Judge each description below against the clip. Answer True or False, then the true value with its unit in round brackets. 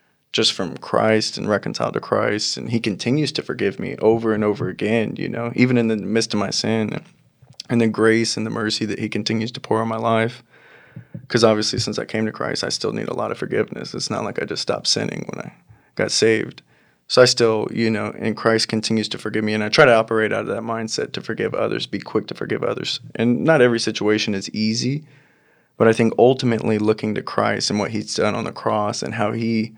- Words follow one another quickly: True (235 wpm)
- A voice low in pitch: True (110 Hz)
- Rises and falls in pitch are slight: True (1.2 semitones)